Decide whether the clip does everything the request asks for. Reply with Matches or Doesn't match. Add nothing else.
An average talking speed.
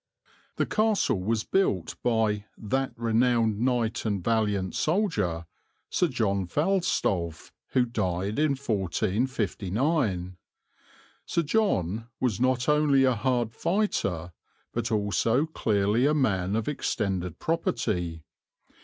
Doesn't match